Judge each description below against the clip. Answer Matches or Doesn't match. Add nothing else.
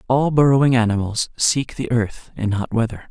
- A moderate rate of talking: Matches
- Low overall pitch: Matches